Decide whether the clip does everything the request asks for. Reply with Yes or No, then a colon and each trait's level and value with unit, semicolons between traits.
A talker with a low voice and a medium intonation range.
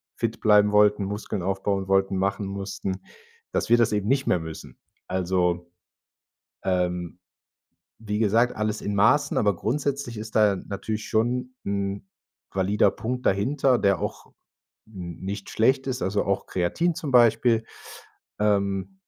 Yes: low, 105 Hz; average, 3.0 semitones